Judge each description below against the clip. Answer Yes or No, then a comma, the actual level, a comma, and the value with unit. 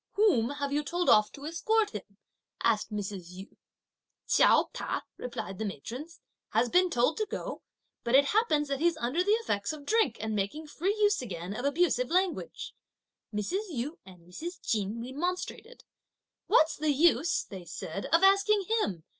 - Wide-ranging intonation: Yes, wide, 9.0 semitones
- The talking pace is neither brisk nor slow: Yes, average, 165 wpm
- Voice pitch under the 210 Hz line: No, very high, 285 Hz